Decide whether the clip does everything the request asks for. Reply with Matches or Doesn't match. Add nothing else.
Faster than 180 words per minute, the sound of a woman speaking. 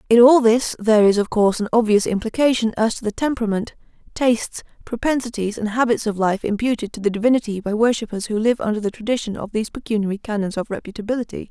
Matches